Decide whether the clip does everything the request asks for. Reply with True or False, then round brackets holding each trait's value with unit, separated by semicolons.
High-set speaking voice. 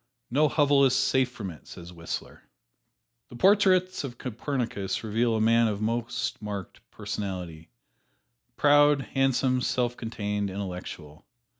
False (115 Hz)